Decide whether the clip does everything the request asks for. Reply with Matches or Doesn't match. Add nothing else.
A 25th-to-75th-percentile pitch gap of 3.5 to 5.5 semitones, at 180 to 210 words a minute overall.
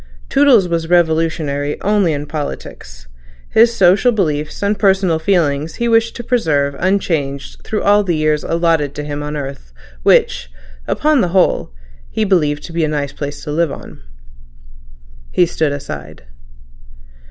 Doesn't match